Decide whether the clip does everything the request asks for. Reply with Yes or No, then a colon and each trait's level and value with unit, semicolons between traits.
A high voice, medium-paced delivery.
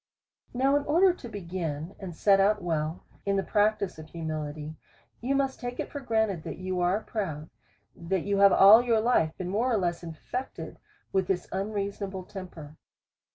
Yes: high, 195 Hz; average, 180 wpm